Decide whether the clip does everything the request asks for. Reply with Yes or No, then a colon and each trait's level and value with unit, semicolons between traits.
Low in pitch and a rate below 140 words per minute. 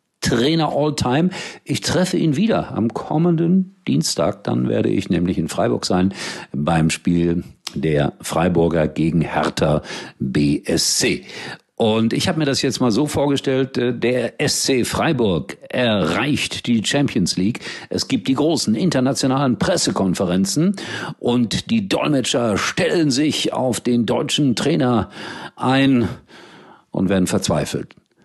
Yes: low, 130 Hz; slow, 125 wpm